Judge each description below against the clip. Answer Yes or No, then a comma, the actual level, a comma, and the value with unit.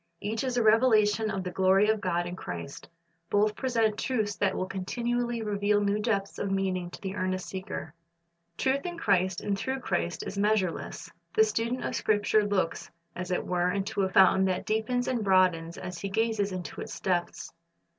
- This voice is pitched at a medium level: No, high, 200 Hz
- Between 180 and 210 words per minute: Yes, average, 185 wpm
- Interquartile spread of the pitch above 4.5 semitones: No, average, 2.9 semitones